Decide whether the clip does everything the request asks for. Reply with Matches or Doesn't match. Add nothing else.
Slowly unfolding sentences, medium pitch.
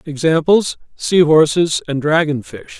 Matches